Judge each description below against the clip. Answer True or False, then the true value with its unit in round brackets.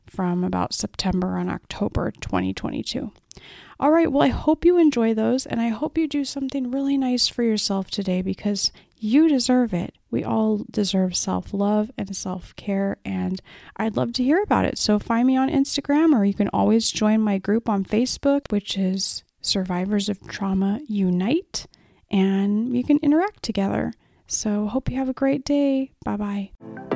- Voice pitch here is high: True (215 Hz)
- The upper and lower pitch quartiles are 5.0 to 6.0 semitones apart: True (5.6 semitones)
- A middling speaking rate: True (175 wpm)